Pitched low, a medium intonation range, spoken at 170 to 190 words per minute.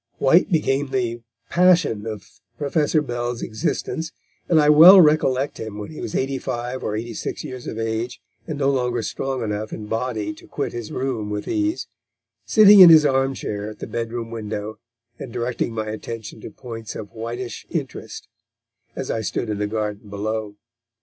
Yes: low, 120 Hz; average, 4.2 semitones; average, 175 wpm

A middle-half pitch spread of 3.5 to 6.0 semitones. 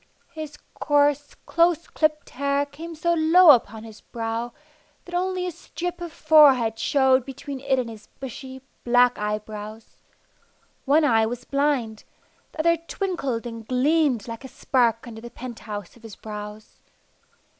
Yes: average, 5.3 semitones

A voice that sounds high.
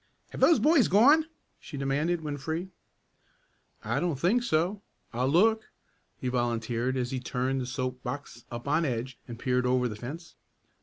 No: low, 135 Hz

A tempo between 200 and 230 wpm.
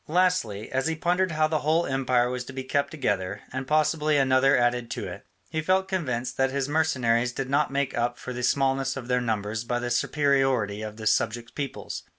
Yes: fast, 205 wpm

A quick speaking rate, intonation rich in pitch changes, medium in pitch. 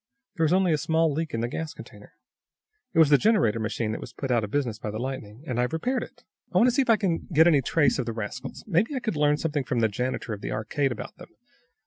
Yes: fast, 275 wpm; wide, 5.8 semitones; medium, 145 Hz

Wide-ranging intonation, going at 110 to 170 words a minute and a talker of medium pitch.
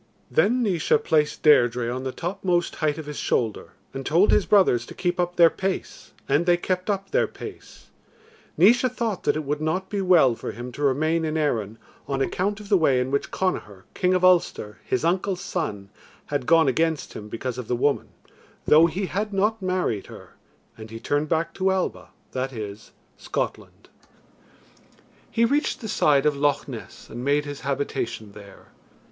No: wide, 6.1 semitones; average, 185 wpm; medium, 155 Hz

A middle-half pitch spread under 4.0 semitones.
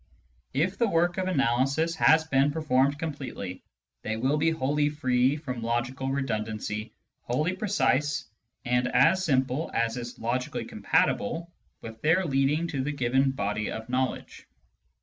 No: average, 4.3 semitones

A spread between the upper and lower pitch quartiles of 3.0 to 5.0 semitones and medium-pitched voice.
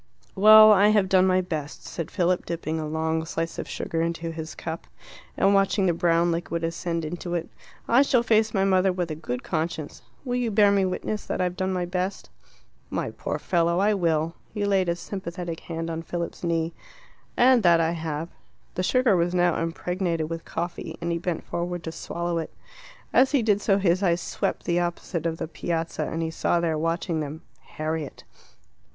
No: narrow, 2.4 semitones; medium, 170 Hz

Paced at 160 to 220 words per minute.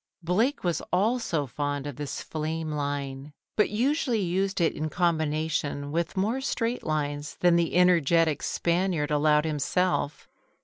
No: slow, 135 wpm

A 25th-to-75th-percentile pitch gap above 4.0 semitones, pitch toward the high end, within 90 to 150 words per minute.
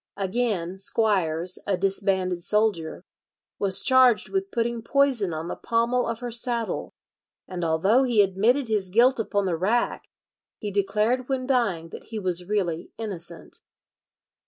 Yes: average, 4.4 semitones; high, 210 Hz; average, 140 wpm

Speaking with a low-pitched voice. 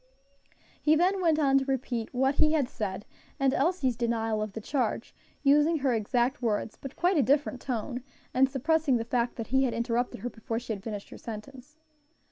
No: very high, 255 Hz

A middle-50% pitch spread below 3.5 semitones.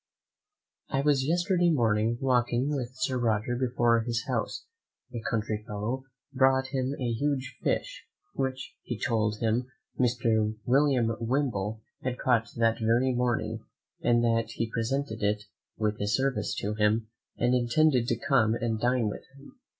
Yes: average, 2.9 semitones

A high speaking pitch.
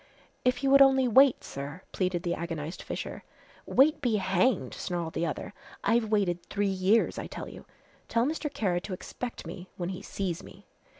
Yes: high, 195 Hz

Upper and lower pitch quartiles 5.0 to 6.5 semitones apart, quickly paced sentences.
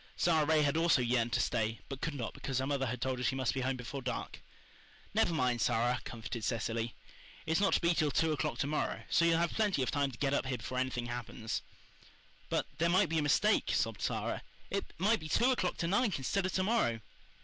Yes: wide, 5.4 semitones; fast, 235 wpm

